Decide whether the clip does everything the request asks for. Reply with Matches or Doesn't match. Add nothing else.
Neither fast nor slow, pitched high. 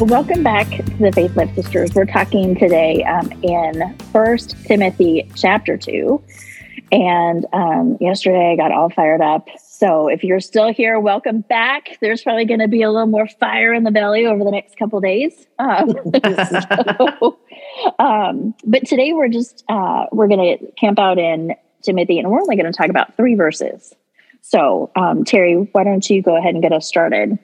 Matches